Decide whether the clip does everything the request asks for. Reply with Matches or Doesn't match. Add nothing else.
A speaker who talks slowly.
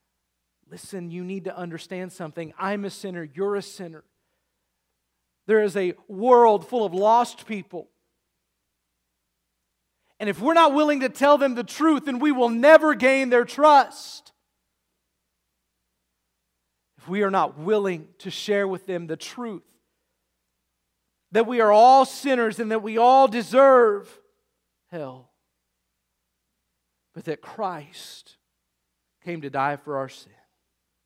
Matches